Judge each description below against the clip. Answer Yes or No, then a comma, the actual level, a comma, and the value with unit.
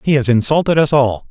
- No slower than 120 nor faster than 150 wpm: No, fast, 230 wpm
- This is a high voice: No, low, 135 Hz